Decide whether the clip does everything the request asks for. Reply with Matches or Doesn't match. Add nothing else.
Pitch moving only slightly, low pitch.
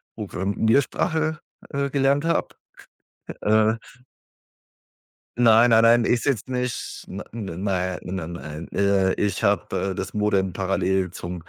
Doesn't match